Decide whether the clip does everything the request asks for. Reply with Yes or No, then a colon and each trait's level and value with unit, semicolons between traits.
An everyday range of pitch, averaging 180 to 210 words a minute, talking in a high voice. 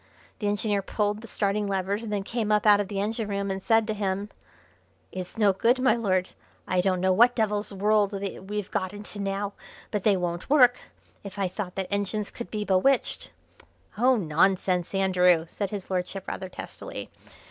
No: narrow, 2.1 semitones; average, 190 wpm; high, 200 Hz